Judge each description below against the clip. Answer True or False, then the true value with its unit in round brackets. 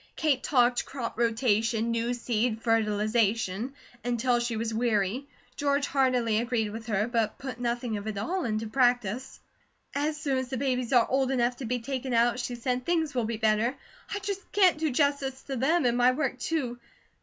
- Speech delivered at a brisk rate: False (185 wpm)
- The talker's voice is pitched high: True (245 Hz)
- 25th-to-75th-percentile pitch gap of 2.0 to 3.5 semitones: True (2.9 semitones)